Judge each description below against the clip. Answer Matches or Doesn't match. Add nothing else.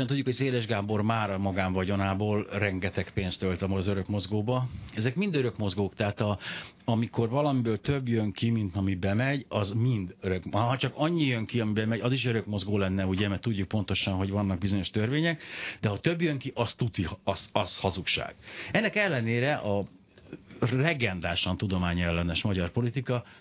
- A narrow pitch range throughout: Doesn't match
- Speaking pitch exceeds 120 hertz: Doesn't match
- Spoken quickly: Matches